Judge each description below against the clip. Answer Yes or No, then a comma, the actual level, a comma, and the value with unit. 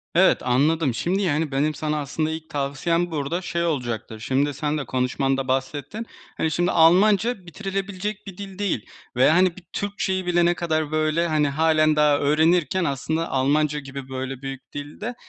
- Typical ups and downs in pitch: Yes, average, 4.1 semitones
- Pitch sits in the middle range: Yes, medium, 155 Hz